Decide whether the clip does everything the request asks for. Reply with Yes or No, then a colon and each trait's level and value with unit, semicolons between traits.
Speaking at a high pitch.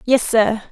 Yes: high, 235 Hz